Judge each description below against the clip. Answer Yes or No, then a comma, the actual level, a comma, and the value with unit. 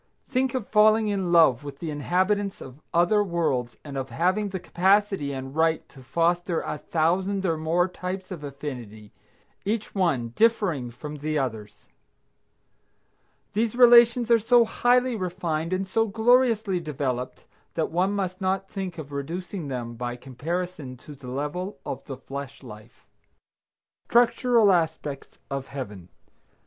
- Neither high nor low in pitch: Yes, medium, 170 Hz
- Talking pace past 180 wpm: No, average, 145 wpm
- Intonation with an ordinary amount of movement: No, wide, 6.3 semitones